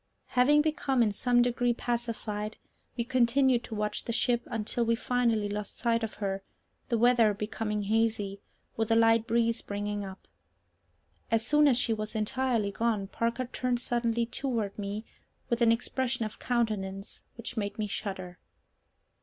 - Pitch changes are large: No, narrow, 2.4 semitones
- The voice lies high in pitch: Yes, high, 230 Hz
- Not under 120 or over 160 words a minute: Yes, average, 155 wpm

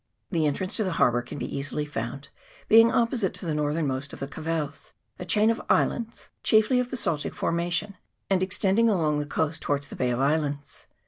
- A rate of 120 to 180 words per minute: No, average, 190 wpm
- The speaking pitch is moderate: Yes, medium, 160 Hz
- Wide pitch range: Yes, wide, 6.2 semitones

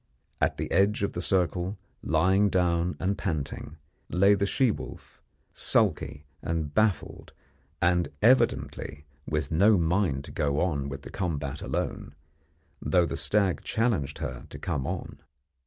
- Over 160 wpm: No, average, 140 wpm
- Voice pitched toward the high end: No, very low, 85 Hz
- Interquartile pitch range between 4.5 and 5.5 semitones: Yes, average, 5.0 semitones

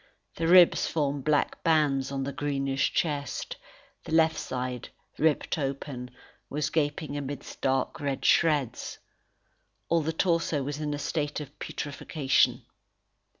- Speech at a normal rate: No, slow, 130 wpm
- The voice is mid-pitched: Yes, medium, 145 Hz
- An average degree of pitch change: No, narrow, 2.3 semitones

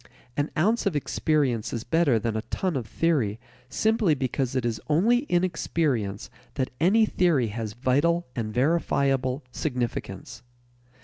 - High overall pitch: No, medium, 140 Hz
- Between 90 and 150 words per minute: Yes, average, 140 wpm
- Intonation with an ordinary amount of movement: No, wide, 6.1 semitones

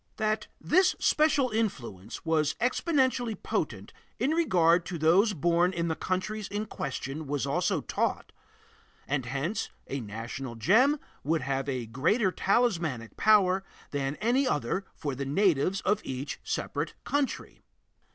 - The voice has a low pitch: No, medium, 170 Hz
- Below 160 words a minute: Yes, slow, 135 wpm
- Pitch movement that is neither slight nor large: No, wide, 7.8 semitones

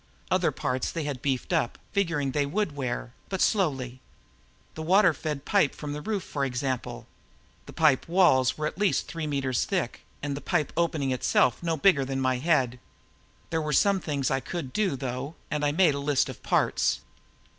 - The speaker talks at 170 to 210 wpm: Yes, average, 190 wpm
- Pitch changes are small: No, average, 4.1 semitones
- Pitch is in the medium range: Yes, medium, 145 Hz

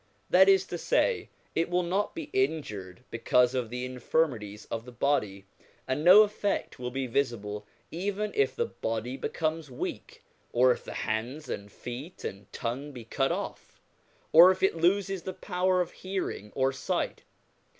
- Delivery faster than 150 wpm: Yes, average, 165 wpm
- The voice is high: No, medium, 140 Hz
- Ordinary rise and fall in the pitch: No, wide, 7.1 semitones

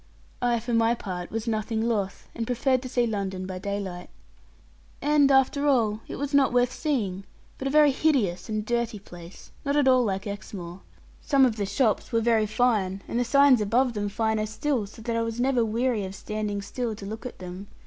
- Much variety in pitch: No, average, 3.9 semitones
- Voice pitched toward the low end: No, high, 225 Hz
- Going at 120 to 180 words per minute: No, fast, 205 wpm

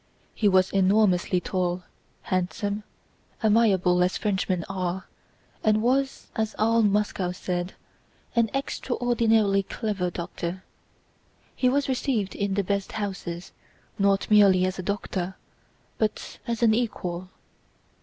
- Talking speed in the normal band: No, slow, 115 wpm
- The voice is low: No, high, 200 Hz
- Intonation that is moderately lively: Yes, average, 3.1 semitones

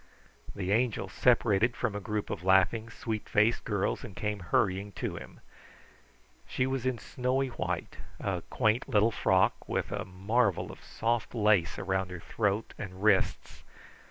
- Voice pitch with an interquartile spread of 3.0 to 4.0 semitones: Yes, average, 3.5 semitones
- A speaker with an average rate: Yes, average, 155 wpm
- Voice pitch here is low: Yes, low, 105 Hz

